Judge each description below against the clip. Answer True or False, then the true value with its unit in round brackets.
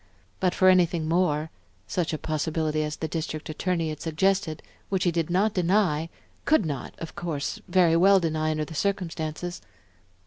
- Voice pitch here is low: False (165 Hz)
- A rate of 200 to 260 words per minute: False (165 wpm)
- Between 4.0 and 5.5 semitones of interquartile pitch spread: False (2.8 semitones)